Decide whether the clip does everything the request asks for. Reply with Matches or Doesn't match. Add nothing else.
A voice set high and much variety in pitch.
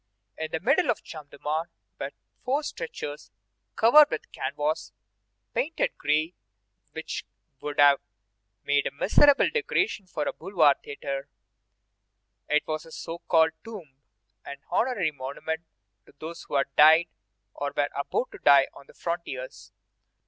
Doesn't match